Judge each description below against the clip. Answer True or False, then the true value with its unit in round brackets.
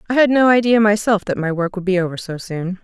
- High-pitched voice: True (200 Hz)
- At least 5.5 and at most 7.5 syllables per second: True (6.0 syllables/s)